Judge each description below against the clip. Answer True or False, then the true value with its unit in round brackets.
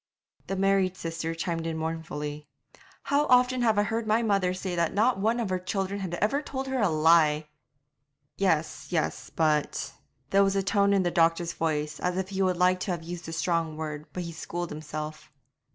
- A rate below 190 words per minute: False (200 wpm)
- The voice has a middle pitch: True (175 Hz)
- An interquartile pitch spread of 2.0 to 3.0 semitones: False (3.6 semitones)